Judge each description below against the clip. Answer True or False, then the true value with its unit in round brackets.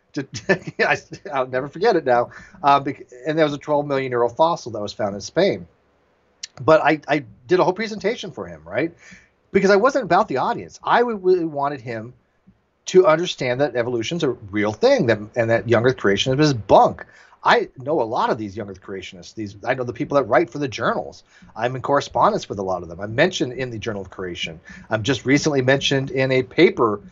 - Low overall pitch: True (130 Hz)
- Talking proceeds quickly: True (215 wpm)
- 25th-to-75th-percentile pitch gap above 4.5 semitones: True (5.6 semitones)